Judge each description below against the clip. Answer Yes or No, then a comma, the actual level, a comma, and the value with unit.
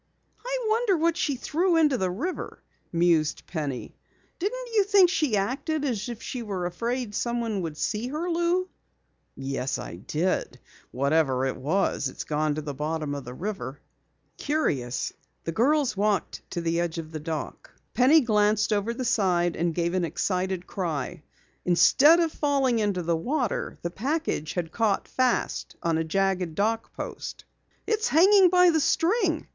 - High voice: Yes, high, 205 Hz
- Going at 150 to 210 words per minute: Yes, average, 160 wpm